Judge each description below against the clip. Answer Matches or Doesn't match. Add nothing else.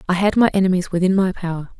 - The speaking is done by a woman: Matches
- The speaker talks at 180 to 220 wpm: Doesn't match